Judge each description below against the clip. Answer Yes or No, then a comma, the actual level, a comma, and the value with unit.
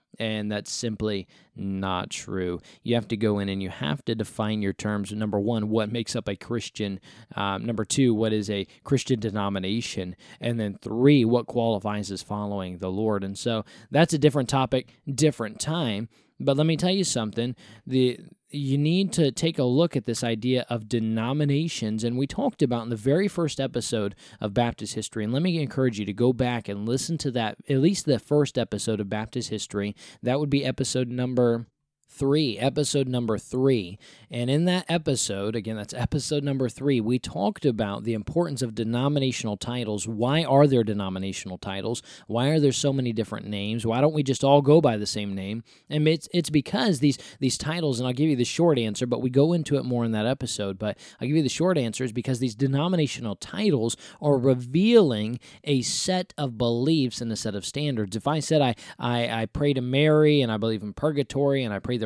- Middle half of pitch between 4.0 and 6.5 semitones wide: Yes, average, 4.8 semitones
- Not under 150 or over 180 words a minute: No, fast, 205 wpm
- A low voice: Yes, low, 120 Hz